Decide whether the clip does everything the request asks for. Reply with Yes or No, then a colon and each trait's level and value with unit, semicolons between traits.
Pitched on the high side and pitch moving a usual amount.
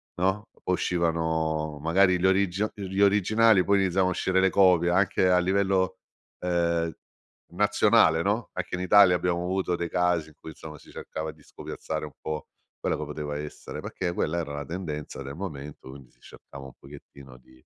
No: very low, 85 Hz; average, 3.4 semitones